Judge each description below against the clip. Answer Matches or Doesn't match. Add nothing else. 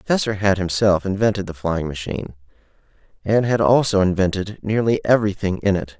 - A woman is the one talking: Doesn't match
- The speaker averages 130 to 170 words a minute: Matches